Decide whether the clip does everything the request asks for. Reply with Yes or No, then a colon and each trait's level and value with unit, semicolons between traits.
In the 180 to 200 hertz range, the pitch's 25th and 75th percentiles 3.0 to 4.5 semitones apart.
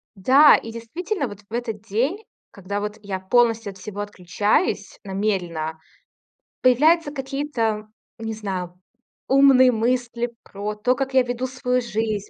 No: high, 225 Hz; average, 4.0 semitones